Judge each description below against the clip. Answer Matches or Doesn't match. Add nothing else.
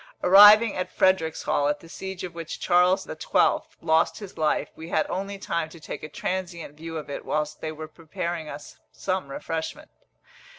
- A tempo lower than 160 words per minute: Doesn't match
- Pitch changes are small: Doesn't match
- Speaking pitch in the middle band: Matches